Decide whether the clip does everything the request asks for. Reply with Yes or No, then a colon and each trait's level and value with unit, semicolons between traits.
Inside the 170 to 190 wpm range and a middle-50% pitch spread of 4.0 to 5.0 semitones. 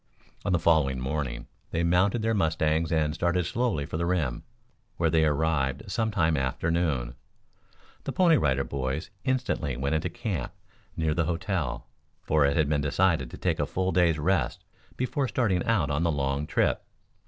Yes: average, 175 wpm; average, 4.3 semitones